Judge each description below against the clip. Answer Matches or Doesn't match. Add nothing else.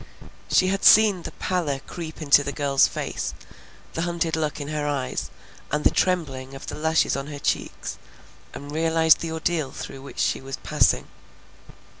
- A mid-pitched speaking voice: Matches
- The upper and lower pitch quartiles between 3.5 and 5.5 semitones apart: Doesn't match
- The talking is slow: Doesn't match